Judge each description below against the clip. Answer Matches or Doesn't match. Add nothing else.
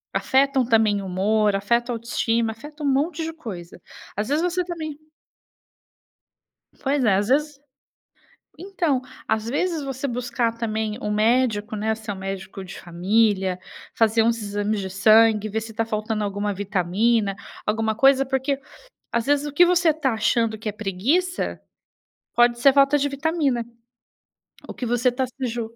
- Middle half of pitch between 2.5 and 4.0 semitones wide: Doesn't match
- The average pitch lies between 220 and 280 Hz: Matches